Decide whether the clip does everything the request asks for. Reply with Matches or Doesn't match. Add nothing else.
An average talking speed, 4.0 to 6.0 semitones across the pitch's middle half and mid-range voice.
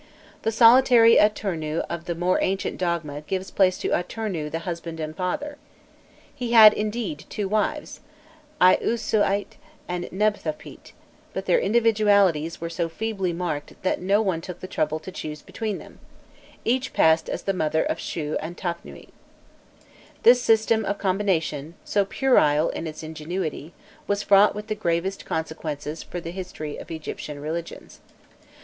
Matches